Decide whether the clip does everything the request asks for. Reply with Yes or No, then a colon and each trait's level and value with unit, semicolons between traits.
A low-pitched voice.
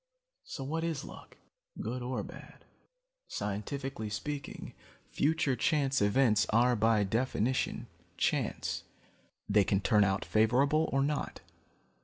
Yes: low, 125 Hz